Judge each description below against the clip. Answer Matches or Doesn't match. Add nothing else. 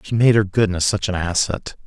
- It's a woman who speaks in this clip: Doesn't match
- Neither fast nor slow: Doesn't match